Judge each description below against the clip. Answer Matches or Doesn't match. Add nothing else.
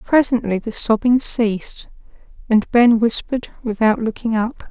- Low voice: Doesn't match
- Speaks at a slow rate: Matches